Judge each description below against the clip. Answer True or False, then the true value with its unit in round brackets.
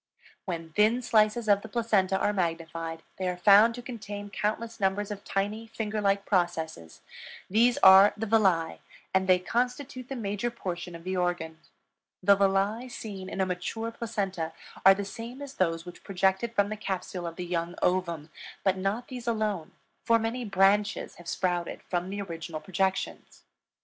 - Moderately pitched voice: False (195 Hz)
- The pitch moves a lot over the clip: False (3.6 semitones)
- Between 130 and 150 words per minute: False (170 wpm)